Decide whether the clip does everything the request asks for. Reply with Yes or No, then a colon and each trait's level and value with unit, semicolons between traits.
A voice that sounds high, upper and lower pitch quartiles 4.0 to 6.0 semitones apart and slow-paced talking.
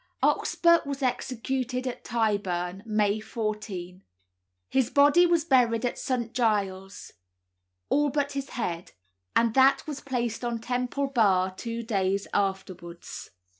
Yes: high, 235 Hz; average, 5.0 semitones; slow, 125 wpm